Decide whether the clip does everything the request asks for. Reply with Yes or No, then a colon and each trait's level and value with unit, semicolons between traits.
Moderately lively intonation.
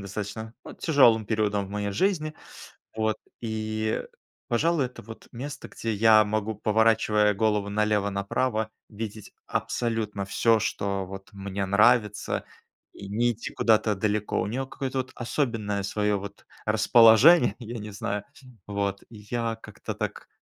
No: narrow, 2.2 semitones